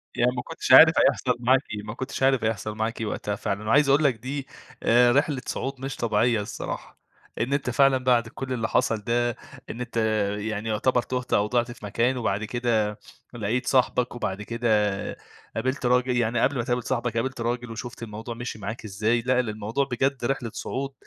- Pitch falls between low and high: No, low, 120 Hz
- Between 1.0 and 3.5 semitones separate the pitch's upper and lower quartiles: Yes, average, 2.7 semitones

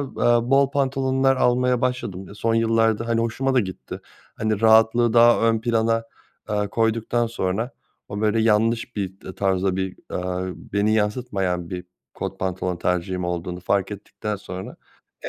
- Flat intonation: No, average, 3.8 semitones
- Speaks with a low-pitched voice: Yes, low, 110 Hz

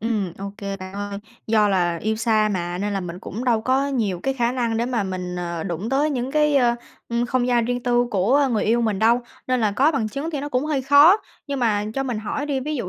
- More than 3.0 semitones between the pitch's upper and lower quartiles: Yes, average, 4.6 semitones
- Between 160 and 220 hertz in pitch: No, high, 235 Hz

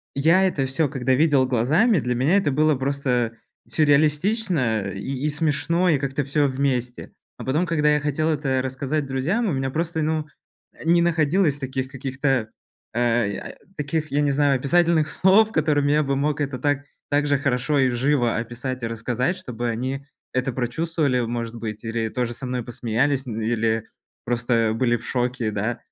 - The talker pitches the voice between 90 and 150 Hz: Yes, low, 135 Hz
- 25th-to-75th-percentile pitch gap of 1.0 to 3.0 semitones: No, average, 3.7 semitones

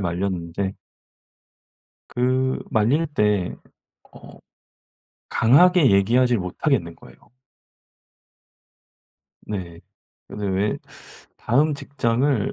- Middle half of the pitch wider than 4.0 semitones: Yes, wide, 5.6 semitones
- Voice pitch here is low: Yes, low, 110 Hz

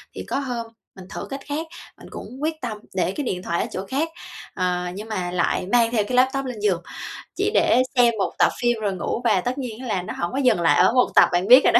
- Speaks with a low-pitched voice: No, high, 235 Hz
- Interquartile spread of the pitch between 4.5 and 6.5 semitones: Yes, wide, 5.5 semitones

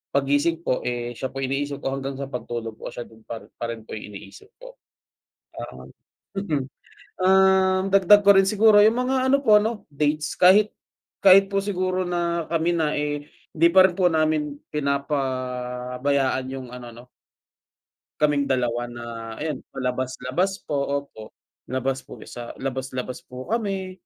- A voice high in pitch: No, medium, 145 Hz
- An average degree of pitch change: No, wide, 6.5 semitones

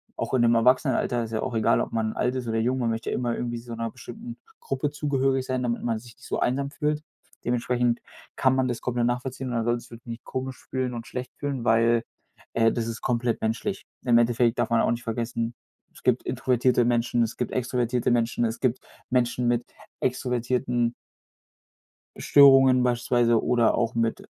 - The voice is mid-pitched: No, low, 120 Hz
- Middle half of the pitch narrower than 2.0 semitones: Yes, narrow, 1.6 semitones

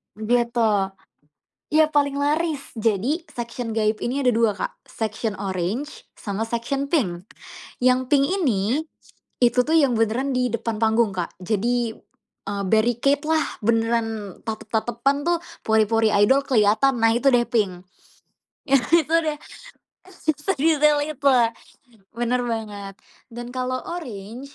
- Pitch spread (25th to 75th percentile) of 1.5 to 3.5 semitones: No, average, 4.1 semitones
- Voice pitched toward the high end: Yes, high, 240 Hz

